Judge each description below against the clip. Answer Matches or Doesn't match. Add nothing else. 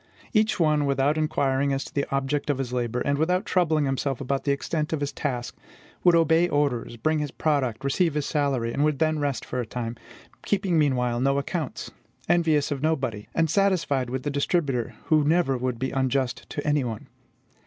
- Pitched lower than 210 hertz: Matches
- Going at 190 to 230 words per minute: Matches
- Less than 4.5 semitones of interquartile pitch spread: Matches